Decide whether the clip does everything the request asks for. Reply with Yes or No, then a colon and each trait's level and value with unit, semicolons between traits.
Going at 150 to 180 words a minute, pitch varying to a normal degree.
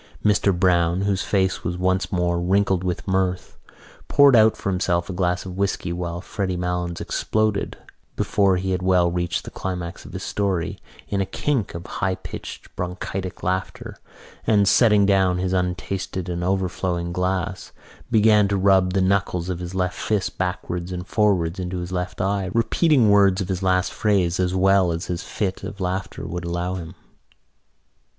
No: average, 170 wpm; narrow, 1.7 semitones